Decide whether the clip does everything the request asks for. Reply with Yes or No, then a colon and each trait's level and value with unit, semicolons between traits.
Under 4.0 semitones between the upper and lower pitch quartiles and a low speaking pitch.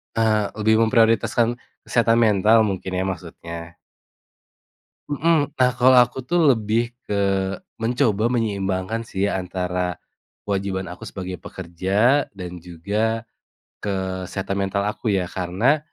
Yes: average, 3.6 semitones; low, 100 Hz